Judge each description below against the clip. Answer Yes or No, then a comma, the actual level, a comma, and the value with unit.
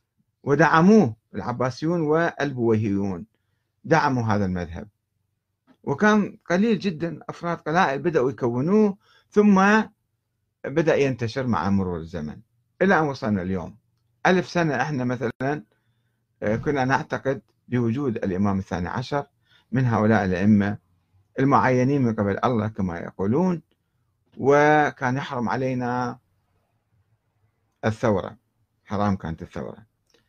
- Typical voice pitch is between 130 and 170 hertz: No, low, 115 Hz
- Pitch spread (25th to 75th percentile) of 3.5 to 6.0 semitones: Yes, average, 5.0 semitones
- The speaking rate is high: No, average, 95 wpm